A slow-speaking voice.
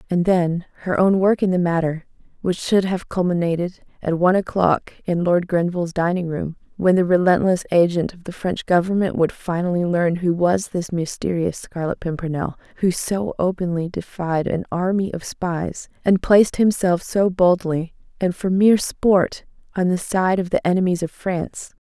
No: average, 170 wpm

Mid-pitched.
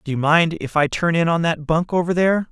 Yes: medium, 165 Hz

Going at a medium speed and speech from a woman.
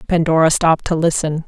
Yes: average, 160 wpm; female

